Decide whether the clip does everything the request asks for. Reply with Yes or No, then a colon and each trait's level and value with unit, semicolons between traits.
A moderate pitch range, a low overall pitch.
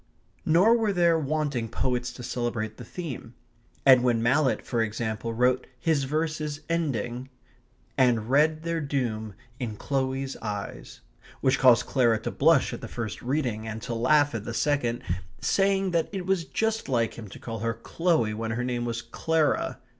Yes: average, 5.0 semitones; low, 130 Hz